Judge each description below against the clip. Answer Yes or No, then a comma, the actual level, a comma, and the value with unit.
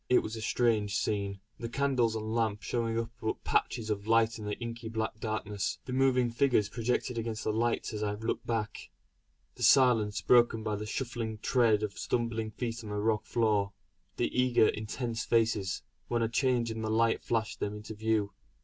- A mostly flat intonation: Yes, narrow, 1.7 semitones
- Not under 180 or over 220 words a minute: Yes, average, 190 wpm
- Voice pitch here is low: Yes, low, 110 Hz